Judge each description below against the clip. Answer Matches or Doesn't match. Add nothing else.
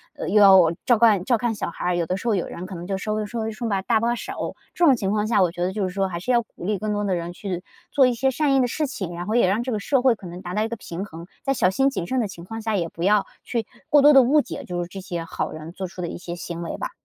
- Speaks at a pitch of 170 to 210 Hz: Matches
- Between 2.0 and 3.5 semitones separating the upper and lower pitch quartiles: Doesn't match